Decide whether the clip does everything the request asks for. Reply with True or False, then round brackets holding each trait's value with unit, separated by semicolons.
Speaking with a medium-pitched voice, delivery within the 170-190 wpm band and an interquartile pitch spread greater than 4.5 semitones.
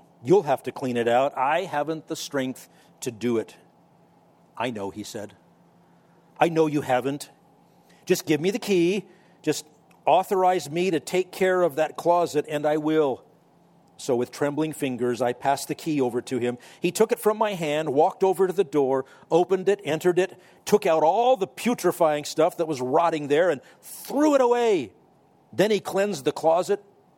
True (160 Hz; 185 wpm; 5.1 semitones)